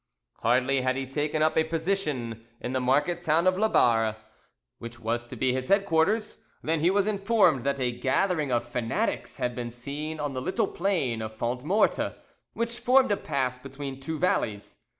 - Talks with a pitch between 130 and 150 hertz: Yes, medium, 140 Hz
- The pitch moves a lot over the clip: Yes, wide, 6.1 semitones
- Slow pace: No, average, 175 wpm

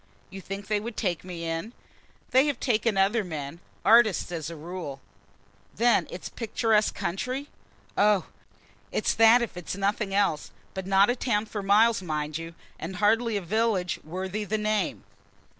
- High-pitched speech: Yes, high, 200 Hz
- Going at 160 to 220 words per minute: Yes, average, 165 wpm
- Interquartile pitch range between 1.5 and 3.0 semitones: No, average, 3.9 semitones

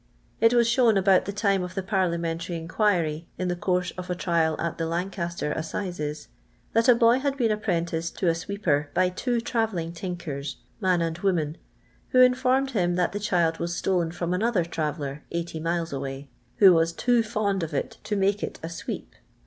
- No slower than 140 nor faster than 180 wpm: No, average, 195 wpm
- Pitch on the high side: No, medium, 180 Hz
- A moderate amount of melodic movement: Yes, average, 3.9 semitones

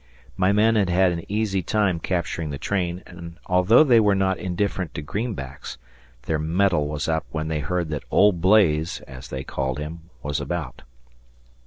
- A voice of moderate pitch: No, very low, 85 Hz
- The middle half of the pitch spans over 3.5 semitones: Yes, average, 4.1 semitones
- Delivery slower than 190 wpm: Yes, average, 175 wpm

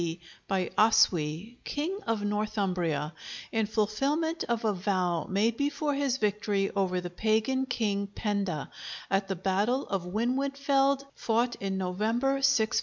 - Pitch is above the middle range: Yes, high, 215 Hz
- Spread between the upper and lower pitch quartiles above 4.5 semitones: Yes, average, 4.9 semitones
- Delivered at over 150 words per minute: No, slow, 135 wpm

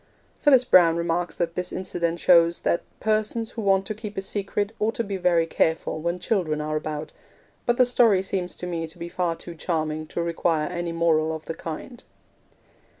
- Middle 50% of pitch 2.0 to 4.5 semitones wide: Yes, average, 3.3 semitones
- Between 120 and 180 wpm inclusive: No, average, 195 wpm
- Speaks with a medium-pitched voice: Yes, medium, 175 Hz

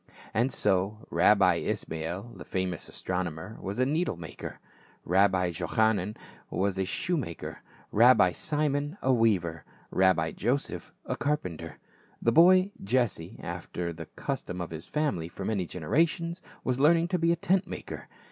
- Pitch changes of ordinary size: No, wide, 8.4 semitones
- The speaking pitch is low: Yes, low, 100 Hz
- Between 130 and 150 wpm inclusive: Yes, average, 145 wpm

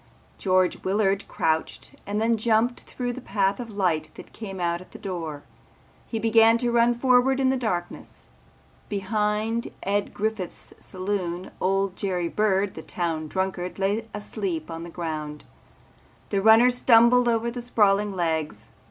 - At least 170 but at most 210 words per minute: No, average, 150 wpm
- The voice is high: Yes, high, 200 Hz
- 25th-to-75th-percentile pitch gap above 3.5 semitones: Yes, average, 4.1 semitones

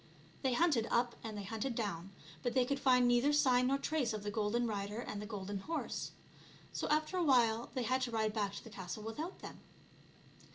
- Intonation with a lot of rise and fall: No, average, 3.9 semitones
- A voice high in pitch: Yes, high, 235 Hz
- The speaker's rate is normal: No, fast, 210 wpm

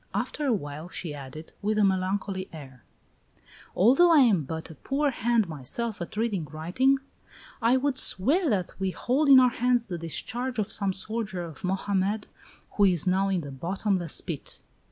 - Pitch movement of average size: No, wide, 5.8 semitones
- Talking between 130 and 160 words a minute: No, average, 175 wpm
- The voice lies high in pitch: Yes, high, 195 Hz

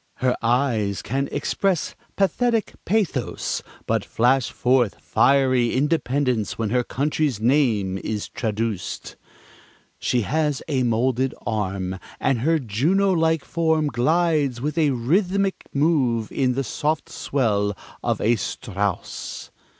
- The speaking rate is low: Yes, slow, 120 wpm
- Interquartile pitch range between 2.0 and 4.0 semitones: No, average, 5.3 semitones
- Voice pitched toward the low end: Yes, low, 130 Hz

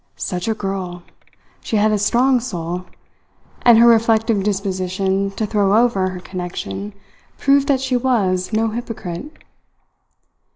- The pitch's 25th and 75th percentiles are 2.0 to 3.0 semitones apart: No, average, 3.8 semitones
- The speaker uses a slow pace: Yes, slow, 130 wpm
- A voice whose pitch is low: No, high, 210 Hz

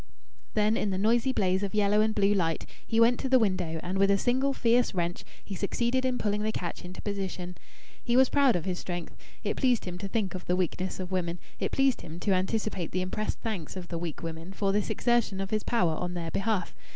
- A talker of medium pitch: No, high, 195 Hz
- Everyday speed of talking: No, fast, 235 wpm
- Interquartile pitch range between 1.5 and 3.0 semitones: No, average, 3.8 semitones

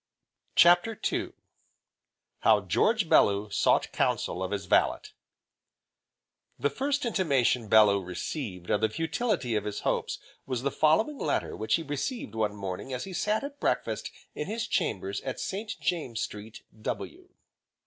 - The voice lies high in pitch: No, low, 130 Hz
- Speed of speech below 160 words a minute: Yes, average, 145 wpm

